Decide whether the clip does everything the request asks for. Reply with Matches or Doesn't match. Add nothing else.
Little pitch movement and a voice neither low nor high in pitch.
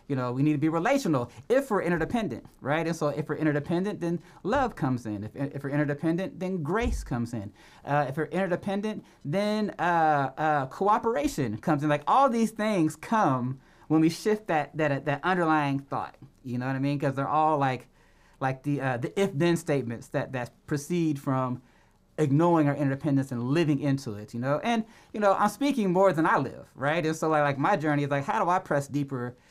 Doesn't match